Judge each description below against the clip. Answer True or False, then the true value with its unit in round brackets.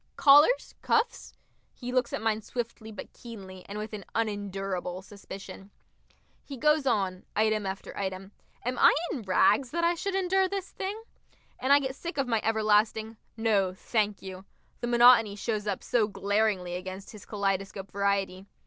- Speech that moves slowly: False (160 wpm)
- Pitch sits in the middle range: False (215 Hz)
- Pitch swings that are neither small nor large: True (4.2 semitones)